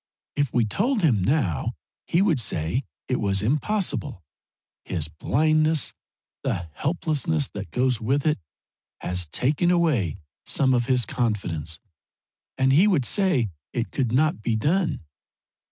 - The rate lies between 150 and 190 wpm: No, slow, 135 wpm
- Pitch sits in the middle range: No, low, 130 Hz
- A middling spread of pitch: No, wide, 6.8 semitones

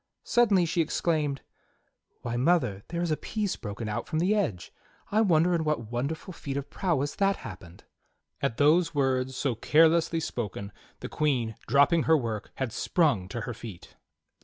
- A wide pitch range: Yes, wide, 6.2 semitones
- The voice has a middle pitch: Yes, medium, 145 Hz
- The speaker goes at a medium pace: Yes, average, 165 wpm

